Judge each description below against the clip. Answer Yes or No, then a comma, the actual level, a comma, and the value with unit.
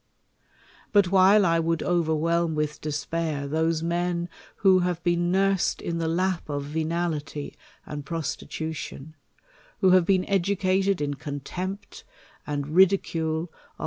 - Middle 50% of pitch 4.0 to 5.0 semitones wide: No, average, 3.0 semitones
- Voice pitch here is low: No, medium, 170 Hz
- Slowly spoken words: Yes, slow, 125 wpm